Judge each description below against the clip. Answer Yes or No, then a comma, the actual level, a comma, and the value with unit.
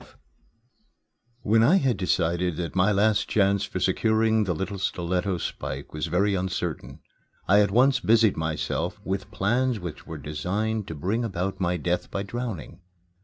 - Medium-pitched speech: No, very low, 95 Hz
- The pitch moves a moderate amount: Yes, average, 3.8 semitones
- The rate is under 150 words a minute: No, average, 155 wpm